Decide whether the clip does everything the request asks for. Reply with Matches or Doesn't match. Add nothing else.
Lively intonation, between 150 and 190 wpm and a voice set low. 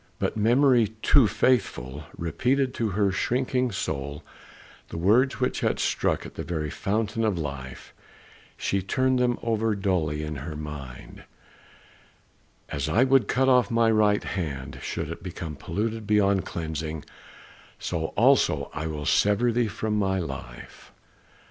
Doesn't match